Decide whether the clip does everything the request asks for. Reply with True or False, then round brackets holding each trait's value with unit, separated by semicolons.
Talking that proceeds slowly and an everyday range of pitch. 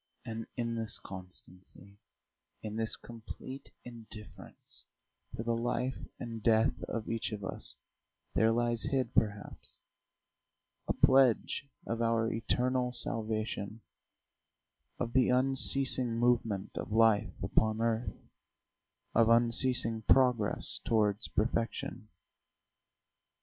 False (100 wpm; 1.8 semitones)